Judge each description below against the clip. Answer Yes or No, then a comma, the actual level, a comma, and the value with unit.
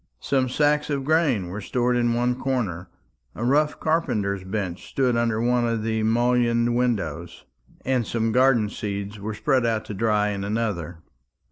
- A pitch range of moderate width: Yes, average, 3.3 semitones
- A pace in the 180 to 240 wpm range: No, average, 160 wpm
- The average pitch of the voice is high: No, low, 115 Hz